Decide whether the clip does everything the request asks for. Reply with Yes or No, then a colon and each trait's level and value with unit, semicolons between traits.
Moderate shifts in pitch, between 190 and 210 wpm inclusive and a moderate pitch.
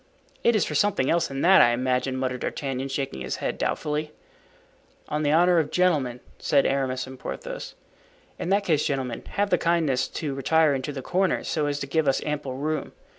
Yes: average, 3.8 semitones; average, 195 wpm; medium, 145 Hz